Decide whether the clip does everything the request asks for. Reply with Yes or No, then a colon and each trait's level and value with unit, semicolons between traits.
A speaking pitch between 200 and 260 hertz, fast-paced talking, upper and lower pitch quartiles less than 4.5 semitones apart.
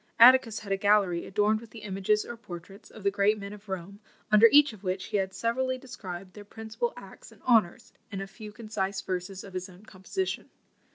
Yes: high, 205 Hz; fast, 210 wpm; narrow, 2.6 semitones